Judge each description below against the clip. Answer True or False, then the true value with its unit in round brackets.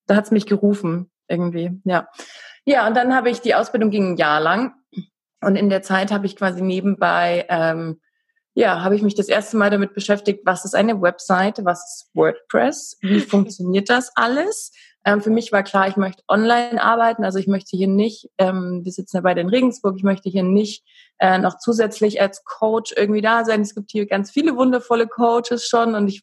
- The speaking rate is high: True (205 wpm)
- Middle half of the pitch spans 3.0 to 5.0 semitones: True (3.4 semitones)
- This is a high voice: True (205 Hz)